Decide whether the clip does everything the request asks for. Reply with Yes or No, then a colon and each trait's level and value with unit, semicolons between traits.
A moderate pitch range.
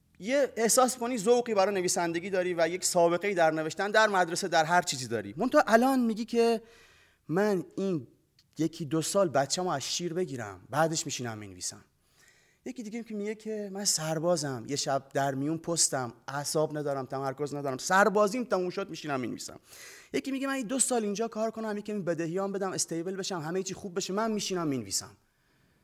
No: wide, 6.3 semitones